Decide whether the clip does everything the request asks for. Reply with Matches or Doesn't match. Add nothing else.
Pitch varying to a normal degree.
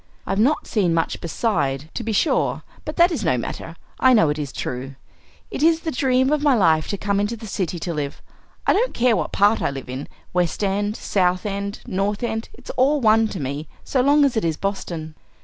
Doesn't match